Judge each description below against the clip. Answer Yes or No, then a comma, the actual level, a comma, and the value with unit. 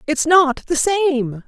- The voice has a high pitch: Yes, very high, 300 Hz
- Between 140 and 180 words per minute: Yes, average, 165 wpm